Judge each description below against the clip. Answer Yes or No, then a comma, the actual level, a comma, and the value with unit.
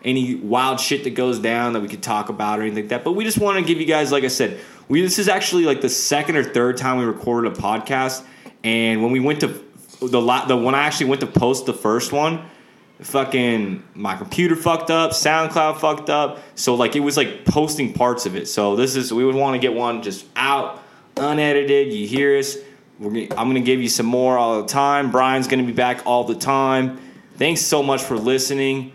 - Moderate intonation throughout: Yes, average, 3.3 semitones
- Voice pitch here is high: No, low, 130 Hz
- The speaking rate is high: Yes, fast, 235 wpm